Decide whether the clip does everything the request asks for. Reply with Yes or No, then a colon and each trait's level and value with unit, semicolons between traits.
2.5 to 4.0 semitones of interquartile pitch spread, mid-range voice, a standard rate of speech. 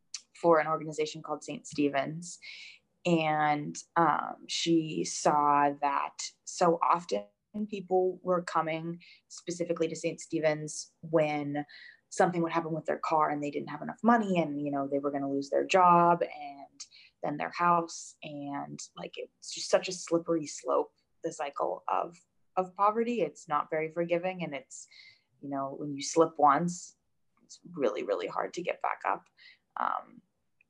Yes: average, 3.2 semitones; medium, 165 Hz; average, 155 wpm